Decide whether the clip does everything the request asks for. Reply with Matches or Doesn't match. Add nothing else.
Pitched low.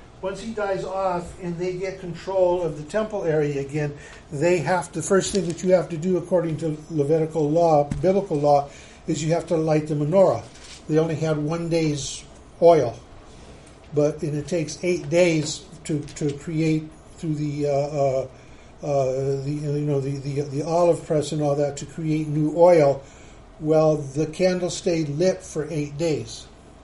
Doesn't match